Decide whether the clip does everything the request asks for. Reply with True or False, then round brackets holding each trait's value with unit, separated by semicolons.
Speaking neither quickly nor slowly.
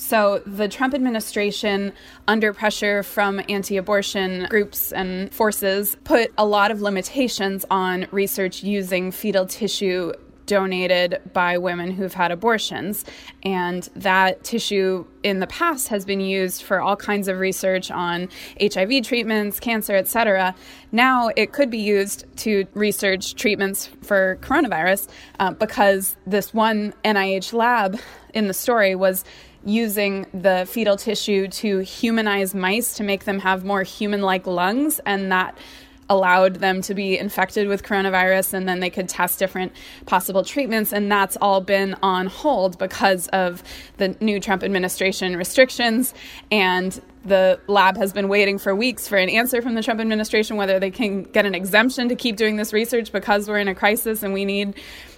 True (160 wpm)